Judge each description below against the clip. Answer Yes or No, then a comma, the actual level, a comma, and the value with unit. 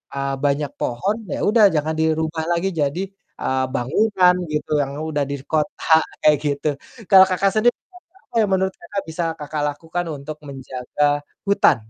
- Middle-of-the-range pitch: Yes, medium, 155 Hz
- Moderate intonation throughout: Yes, average, 4.6 semitones